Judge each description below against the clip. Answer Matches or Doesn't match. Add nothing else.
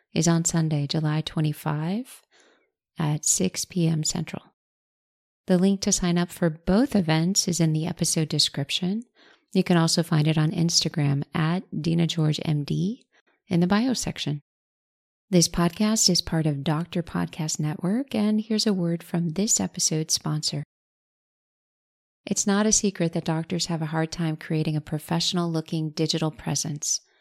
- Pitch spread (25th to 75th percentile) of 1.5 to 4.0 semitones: Matches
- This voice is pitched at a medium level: Matches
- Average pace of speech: Matches